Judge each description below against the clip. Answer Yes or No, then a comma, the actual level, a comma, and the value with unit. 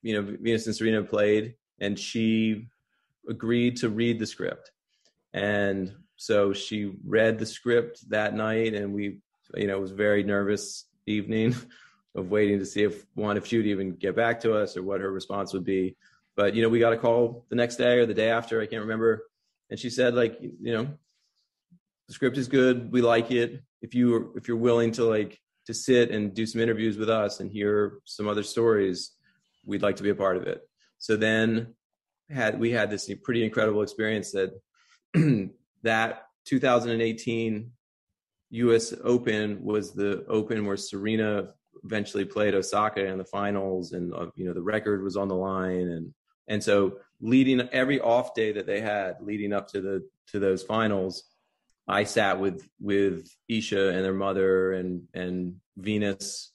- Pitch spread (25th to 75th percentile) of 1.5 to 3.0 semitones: Yes, narrow, 2.6 semitones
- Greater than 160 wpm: Yes, average, 185 wpm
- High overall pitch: No, low, 110 Hz